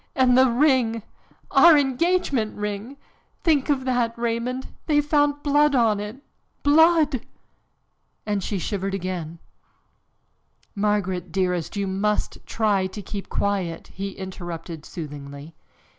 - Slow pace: Yes, slow, 115 wpm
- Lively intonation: Yes, wide, 6.1 semitones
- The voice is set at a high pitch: Yes, high, 215 Hz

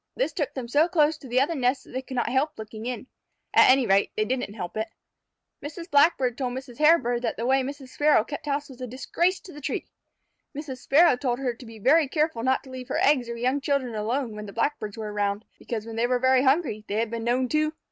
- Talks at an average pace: No, fast, 250 wpm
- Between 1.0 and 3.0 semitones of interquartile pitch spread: No, average, 3.7 semitones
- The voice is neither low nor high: No, very high, 255 Hz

